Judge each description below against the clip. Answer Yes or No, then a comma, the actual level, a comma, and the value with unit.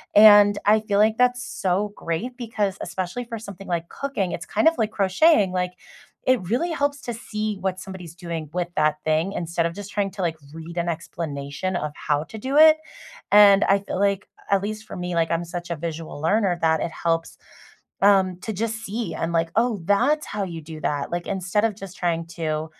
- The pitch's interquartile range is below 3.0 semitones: No, average, 4.2 semitones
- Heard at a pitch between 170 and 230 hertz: Yes, high, 190 Hz